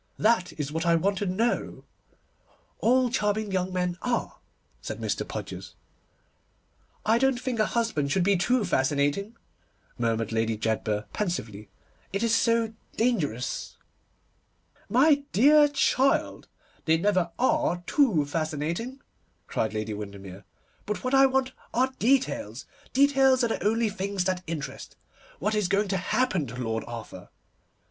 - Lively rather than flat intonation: Yes, wide, 8.7 semitones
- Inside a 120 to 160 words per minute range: Yes, average, 140 wpm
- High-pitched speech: Yes, high, 195 Hz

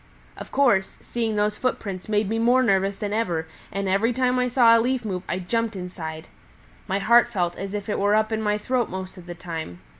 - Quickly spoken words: Yes, fast, 220 wpm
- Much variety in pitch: No, average, 3.6 semitones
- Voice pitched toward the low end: No, high, 210 Hz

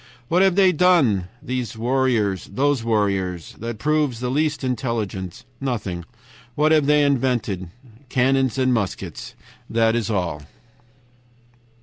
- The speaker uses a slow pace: Yes, slow, 110 wpm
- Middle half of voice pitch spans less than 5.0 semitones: No, wide, 5.5 semitones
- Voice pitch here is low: Yes, low, 120 Hz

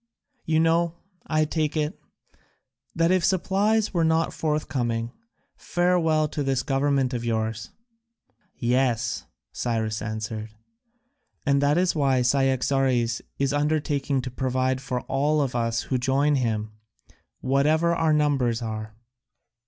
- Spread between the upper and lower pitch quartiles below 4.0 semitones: No, average, 4.4 semitones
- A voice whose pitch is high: No, low, 135 Hz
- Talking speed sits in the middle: No, slow, 120 wpm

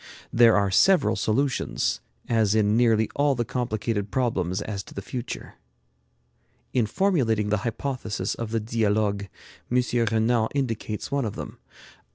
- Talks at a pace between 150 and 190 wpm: No, average, 140 wpm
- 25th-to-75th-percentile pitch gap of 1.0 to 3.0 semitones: Yes, narrow, 2.6 semitones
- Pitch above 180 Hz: No, low, 110 Hz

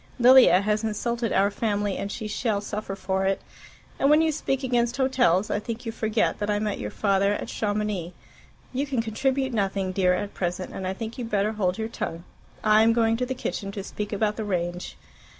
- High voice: Yes, high, 210 Hz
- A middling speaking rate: No, fast, 215 wpm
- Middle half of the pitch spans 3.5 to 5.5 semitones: No, average, 3.0 semitones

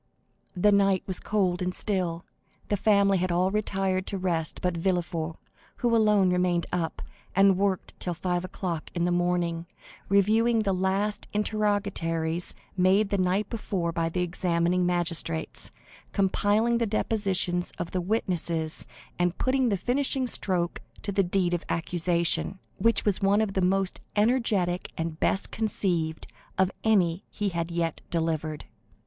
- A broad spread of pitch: No, average, 2.8 semitones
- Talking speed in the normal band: Yes, average, 145 wpm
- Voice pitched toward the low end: No, medium, 185 Hz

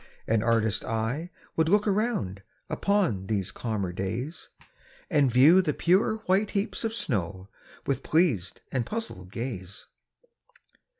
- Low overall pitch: Yes, low, 125 Hz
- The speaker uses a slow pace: Yes, slow, 125 wpm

